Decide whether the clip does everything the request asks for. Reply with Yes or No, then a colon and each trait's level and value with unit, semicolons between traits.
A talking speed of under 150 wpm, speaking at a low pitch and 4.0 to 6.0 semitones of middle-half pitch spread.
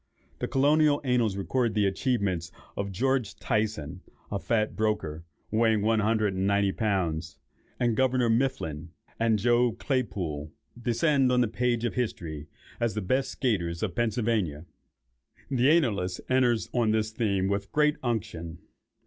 Yes: average, 140 wpm; low, 110 Hz; average, 4.4 semitones